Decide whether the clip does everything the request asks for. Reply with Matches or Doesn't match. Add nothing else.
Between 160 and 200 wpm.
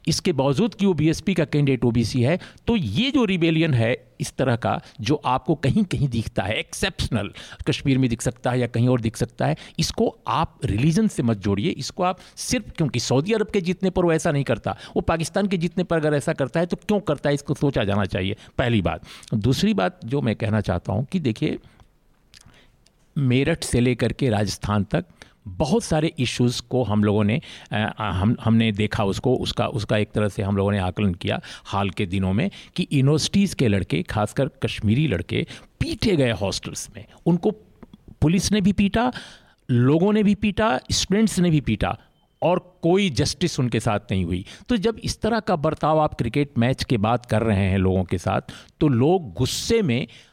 Matches